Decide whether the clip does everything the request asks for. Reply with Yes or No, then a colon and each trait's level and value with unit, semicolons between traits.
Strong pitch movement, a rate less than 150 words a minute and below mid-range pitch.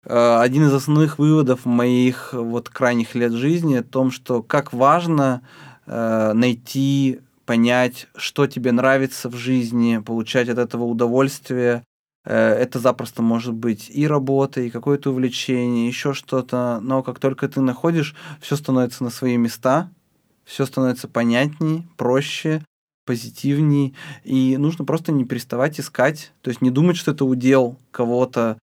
No: narrow, 2.6 semitones; average, 135 wpm; low, 130 Hz